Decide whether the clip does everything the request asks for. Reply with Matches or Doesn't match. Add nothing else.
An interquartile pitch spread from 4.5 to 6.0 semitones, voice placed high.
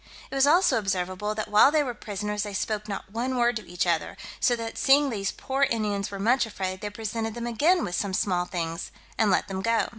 Doesn't match